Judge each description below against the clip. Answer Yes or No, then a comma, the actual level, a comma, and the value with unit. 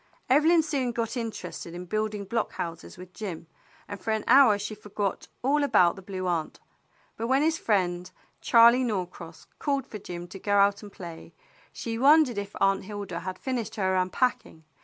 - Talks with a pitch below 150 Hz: No, high, 205 Hz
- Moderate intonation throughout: Yes, average, 4.6 semitones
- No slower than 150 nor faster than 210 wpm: Yes, average, 180 wpm